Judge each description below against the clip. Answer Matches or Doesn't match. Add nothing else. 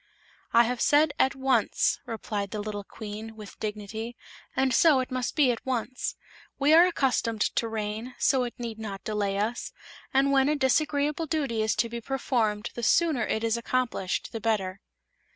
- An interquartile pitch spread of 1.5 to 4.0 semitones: Matches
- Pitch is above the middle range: Matches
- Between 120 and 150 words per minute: Doesn't match